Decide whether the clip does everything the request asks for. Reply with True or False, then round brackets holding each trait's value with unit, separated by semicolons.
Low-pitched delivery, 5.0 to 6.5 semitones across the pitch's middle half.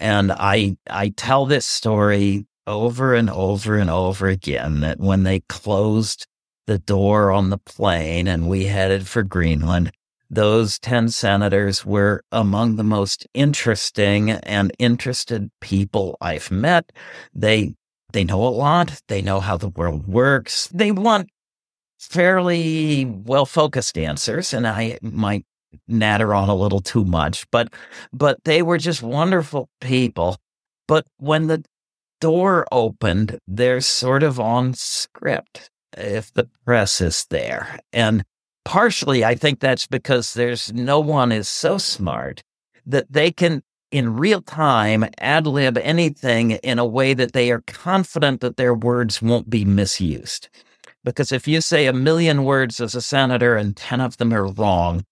True (115 Hz; 5.3 semitones)